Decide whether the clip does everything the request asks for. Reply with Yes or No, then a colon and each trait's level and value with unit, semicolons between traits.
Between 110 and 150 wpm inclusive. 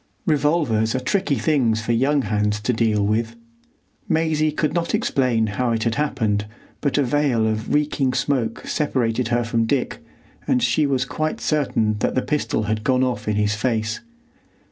No: average, 170 wpm